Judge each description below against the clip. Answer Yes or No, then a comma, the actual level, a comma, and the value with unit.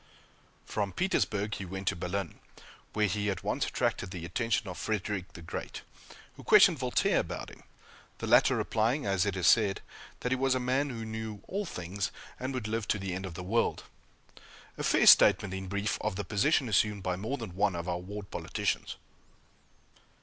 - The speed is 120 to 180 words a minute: No, average, 190 wpm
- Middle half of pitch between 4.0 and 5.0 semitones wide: No, average, 3.2 semitones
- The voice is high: No, low, 105 Hz